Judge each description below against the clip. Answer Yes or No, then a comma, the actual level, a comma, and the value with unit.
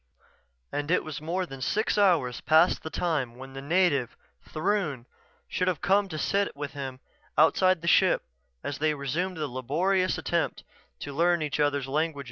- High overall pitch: No, medium, 155 Hz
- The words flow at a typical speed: Yes, average, 170 wpm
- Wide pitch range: No, average, 4.5 semitones